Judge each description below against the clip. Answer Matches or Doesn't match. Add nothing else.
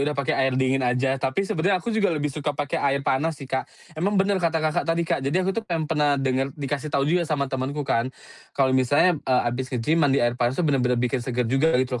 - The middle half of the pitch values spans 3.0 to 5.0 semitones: Matches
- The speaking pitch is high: Doesn't match